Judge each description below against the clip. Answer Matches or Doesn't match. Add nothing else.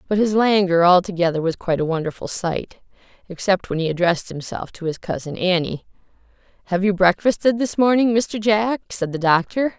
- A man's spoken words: Doesn't match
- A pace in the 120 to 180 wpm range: Matches